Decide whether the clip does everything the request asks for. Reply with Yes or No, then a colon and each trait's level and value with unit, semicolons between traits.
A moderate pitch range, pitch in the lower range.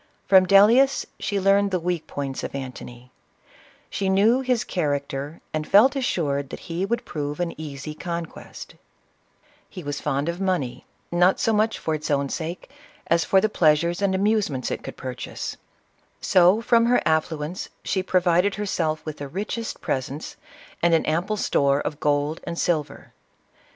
No: average, 5.0 semitones; medium, 170 Hz